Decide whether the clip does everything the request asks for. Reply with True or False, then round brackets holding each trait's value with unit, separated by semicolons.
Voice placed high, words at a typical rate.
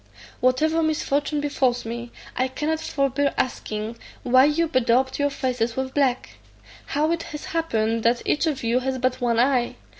True (260 Hz; 160 wpm)